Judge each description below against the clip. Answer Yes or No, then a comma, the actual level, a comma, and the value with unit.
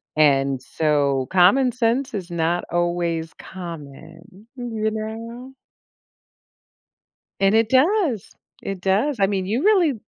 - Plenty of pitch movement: Yes, wide, 6.1 semitones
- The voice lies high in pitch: Yes, high, 195 Hz